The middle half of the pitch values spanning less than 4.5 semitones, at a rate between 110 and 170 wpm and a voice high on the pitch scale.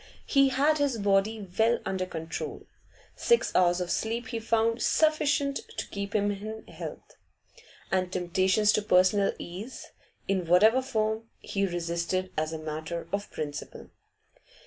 Yes: average, 4.1 semitones; average, 140 wpm; high, 200 Hz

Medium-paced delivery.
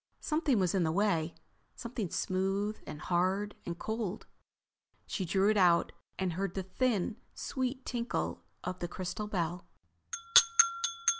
No: slow, 130 wpm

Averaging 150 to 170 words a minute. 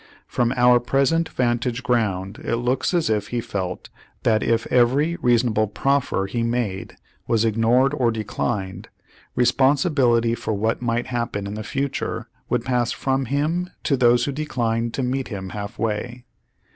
Yes: average, 155 wpm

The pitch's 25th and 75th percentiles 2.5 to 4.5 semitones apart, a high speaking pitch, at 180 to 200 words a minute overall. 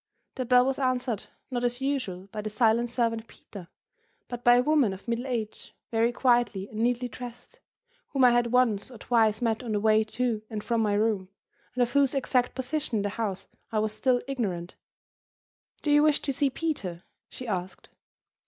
Yes: average, 2.8 semitones; high, 235 Hz; average, 190 wpm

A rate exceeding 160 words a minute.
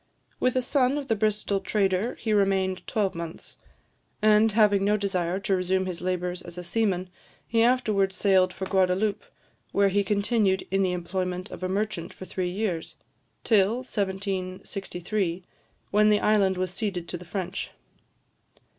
No: average, 155 wpm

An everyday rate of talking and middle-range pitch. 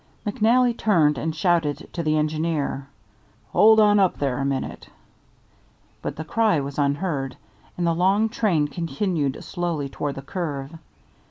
Yes: average, 145 wpm; medium, 160 Hz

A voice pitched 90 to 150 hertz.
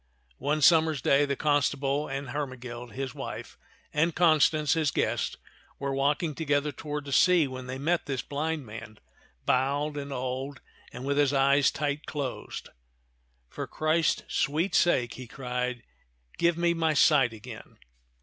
Yes: medium, 140 Hz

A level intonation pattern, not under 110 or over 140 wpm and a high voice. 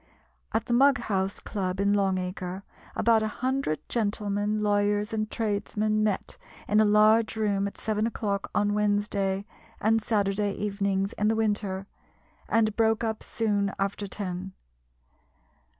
Yes: narrow, 1.6 semitones; slow, 135 wpm; high, 205 Hz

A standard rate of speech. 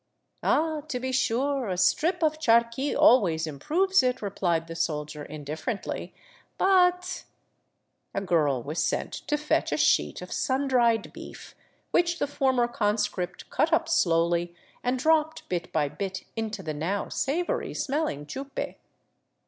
Yes: average, 155 wpm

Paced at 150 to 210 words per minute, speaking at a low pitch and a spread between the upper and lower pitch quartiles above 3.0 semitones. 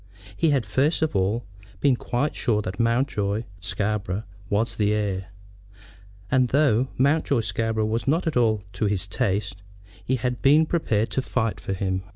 Yes: average, 165 wpm; low, 110 Hz; average, 4.4 semitones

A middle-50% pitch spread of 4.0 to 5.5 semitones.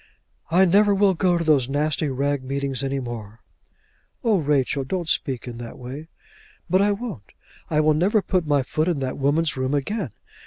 Yes: average, 5.1 semitones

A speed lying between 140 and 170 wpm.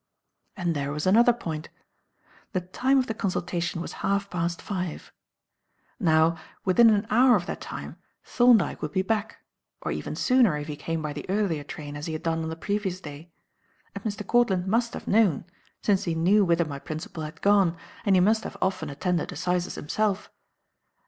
No: average, 185 wpm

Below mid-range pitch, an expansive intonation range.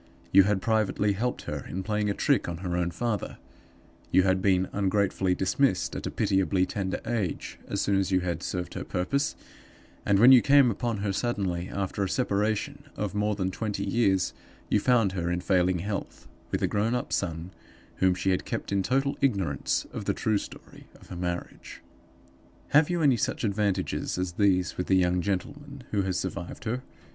No: low, 100 Hz; average, 3.2 semitones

